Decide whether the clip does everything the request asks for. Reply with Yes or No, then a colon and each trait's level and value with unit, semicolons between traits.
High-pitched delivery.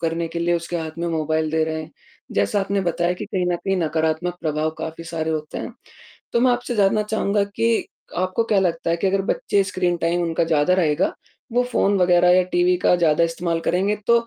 No: medium, 175 Hz